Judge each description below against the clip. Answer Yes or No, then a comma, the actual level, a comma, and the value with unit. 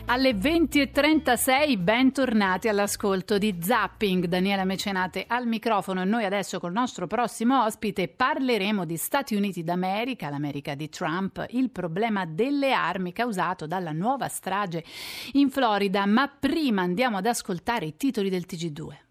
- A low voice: No, high, 205 Hz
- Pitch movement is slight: No, average, 5.1 semitones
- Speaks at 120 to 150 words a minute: Yes, average, 140 wpm